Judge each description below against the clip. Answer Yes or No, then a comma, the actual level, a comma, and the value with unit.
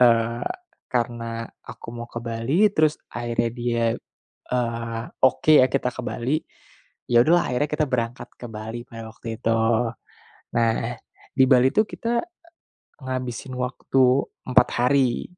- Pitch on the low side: Yes, low, 120 Hz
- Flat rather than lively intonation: Yes, narrow, 2.0 semitones